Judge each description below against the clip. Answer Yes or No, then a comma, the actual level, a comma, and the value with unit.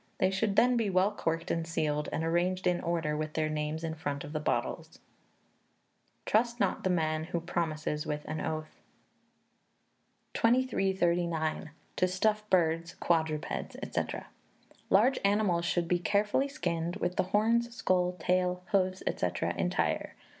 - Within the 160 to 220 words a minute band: No, average, 145 wpm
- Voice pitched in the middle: Yes, medium, 175 Hz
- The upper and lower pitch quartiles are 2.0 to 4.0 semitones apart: Yes, average, 3.5 semitones